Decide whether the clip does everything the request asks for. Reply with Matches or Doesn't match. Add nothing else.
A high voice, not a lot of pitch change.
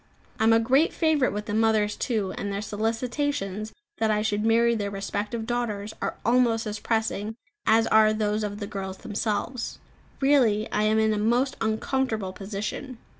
Matches